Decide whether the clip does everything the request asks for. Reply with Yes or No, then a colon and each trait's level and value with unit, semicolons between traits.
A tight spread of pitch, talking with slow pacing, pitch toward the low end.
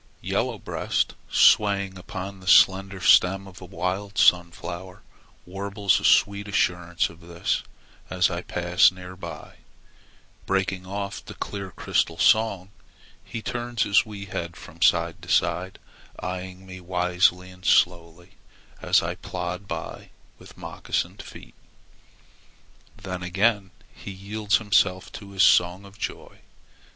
Yes: narrow, 1.8 semitones; slow, 125 wpm; very low, 95 Hz